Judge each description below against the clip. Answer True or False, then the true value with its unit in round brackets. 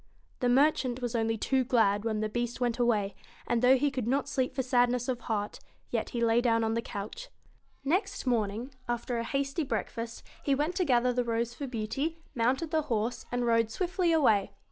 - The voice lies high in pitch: True (245 Hz)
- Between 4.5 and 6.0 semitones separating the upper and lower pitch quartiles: False (3.1 semitones)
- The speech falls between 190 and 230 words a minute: True (205 wpm)